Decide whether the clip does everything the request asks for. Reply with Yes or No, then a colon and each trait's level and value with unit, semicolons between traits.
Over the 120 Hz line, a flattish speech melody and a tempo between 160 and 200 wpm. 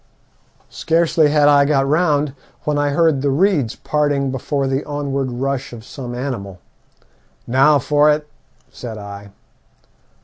No: medium, 140 Hz; narrow, 2.3 semitones; slow, 135 wpm